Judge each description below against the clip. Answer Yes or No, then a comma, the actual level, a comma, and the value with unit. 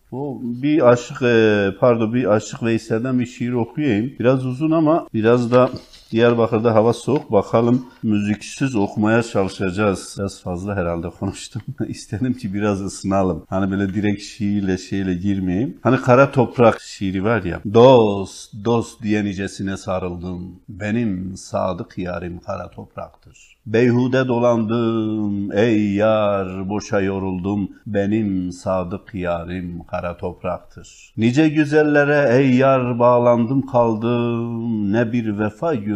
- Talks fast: No, average, 125 wpm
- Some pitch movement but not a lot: Yes, average, 3.7 semitones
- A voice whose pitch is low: Yes, low, 110 Hz